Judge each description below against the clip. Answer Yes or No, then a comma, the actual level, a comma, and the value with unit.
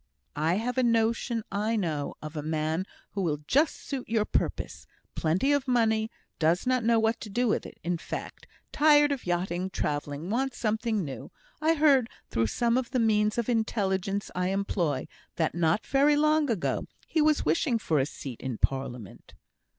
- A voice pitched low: No, high, 215 Hz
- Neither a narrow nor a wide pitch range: No, wide, 6.8 semitones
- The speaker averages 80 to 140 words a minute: No, average, 180 wpm